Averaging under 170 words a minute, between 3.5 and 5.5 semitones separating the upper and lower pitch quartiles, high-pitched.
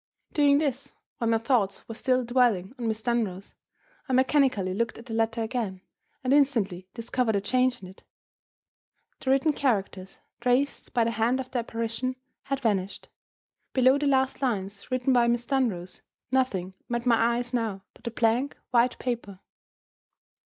No: average, 160 wpm; average, 2.8 semitones; high, 235 Hz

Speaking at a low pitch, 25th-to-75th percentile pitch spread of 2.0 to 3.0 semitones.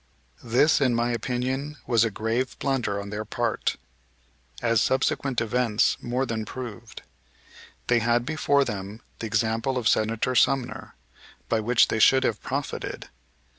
Yes: low, 120 Hz; narrow, 2.6 semitones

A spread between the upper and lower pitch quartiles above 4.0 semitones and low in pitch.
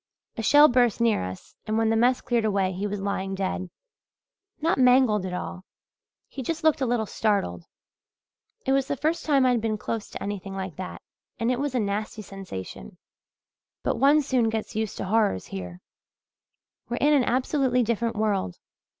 No: average, 4.5 semitones; high, 225 Hz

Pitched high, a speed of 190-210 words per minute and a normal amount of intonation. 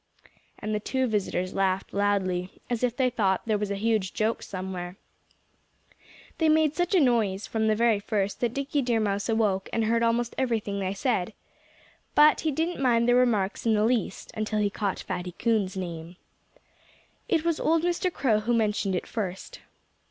No: high, 220 Hz; average, 180 wpm; average, 3.8 semitones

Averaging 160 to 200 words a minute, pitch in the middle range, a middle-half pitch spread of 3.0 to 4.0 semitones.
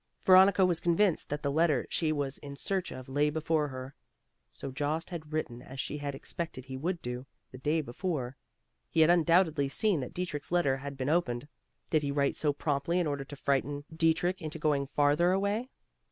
Yes: average, 195 wpm; medium, 150 Hz; average, 3.6 semitones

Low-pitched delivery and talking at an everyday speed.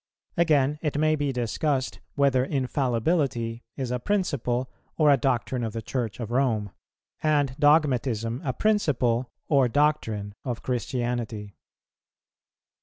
No: low, 130 Hz; slow, 120 wpm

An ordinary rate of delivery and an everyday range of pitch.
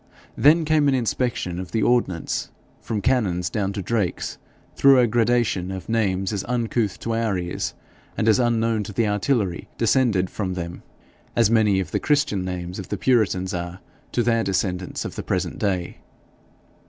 Yes: average, 170 wpm; average, 4.3 semitones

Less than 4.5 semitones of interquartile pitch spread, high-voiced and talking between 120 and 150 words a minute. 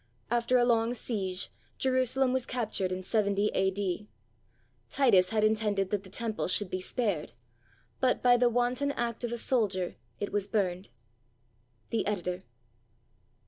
Yes: average, 4.0 semitones; high, 215 Hz; average, 145 wpm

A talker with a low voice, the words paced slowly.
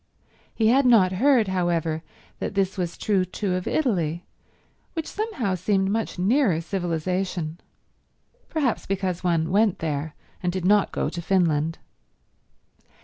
No: medium, 185 Hz; slow, 130 wpm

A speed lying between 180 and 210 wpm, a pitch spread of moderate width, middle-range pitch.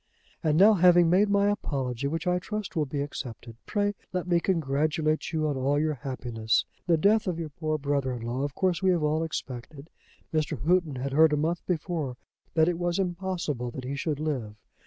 Yes: average, 200 wpm; average, 4.2 semitones; medium, 155 Hz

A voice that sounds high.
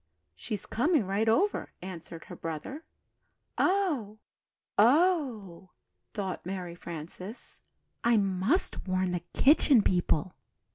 Yes: high, 200 Hz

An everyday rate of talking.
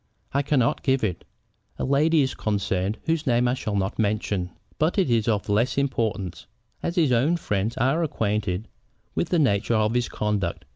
Yes: average, 180 wpm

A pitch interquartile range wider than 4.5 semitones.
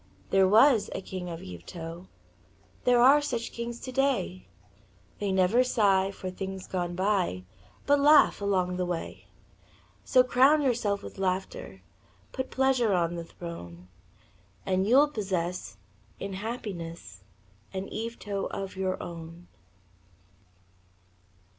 Yes: average, 5.2 semitones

